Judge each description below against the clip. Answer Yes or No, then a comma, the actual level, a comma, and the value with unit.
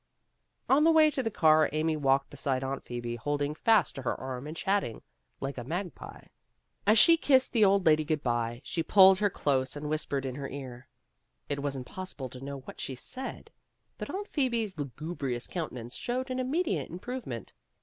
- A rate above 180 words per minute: Yes, average, 200 wpm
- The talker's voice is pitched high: No, medium, 155 Hz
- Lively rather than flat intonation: Yes, wide, 7.7 semitones